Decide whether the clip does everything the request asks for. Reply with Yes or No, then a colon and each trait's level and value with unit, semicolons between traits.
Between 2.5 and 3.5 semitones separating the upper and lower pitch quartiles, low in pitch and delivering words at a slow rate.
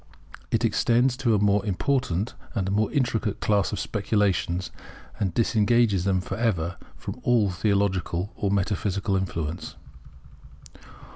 Yes: average, 3.2 semitones; low, 100 Hz; slow, 125 wpm